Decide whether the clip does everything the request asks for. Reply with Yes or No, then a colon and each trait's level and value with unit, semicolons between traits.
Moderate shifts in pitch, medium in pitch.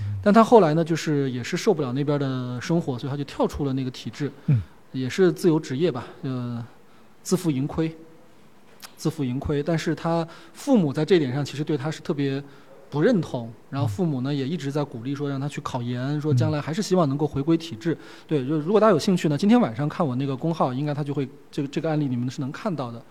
Yes: average, 3.3 semitones; medium, 150 Hz